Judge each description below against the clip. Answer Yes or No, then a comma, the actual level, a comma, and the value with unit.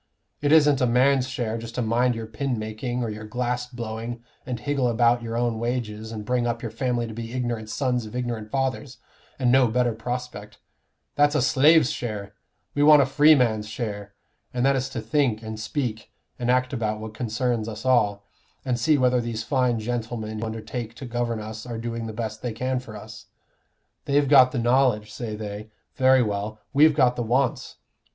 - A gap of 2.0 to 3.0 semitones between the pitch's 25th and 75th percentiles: Yes, narrow, 2.6 semitones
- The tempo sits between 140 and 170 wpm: No, average, 195 wpm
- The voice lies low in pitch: Yes, low, 120 Hz